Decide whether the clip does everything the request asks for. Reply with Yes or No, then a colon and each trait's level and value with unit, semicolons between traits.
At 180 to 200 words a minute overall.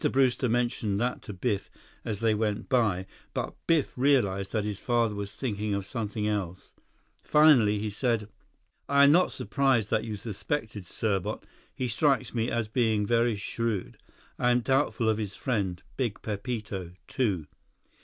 No: average, 155 wpm